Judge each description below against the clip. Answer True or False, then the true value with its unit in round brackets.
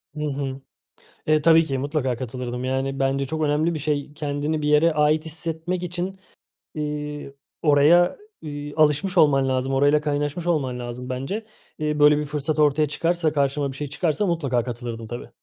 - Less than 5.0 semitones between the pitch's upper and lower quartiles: True (2.5 semitones)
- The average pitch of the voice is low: False (150 Hz)